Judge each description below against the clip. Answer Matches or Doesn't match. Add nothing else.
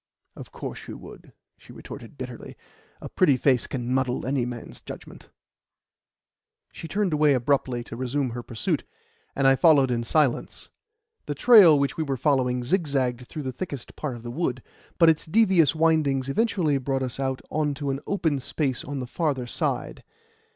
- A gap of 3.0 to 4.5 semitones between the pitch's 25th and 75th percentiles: Matches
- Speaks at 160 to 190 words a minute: Matches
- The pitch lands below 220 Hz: Matches